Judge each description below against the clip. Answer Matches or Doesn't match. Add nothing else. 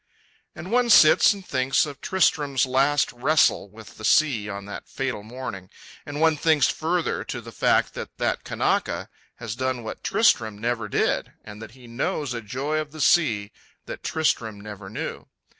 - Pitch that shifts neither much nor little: Doesn't match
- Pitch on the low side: Matches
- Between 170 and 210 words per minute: Matches